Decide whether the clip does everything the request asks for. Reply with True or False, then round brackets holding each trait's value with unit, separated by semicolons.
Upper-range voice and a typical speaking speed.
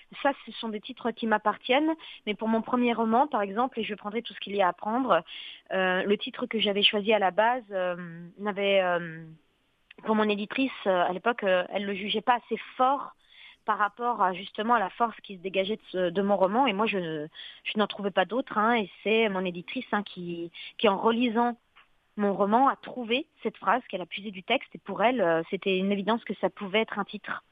False (210 Hz; 235 wpm)